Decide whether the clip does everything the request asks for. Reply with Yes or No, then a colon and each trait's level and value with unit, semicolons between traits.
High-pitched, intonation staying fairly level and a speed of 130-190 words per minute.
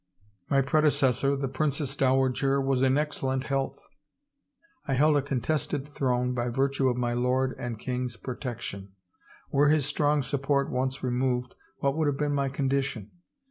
No: low, 135 Hz; narrow, 1.8 semitones; average, 155 wpm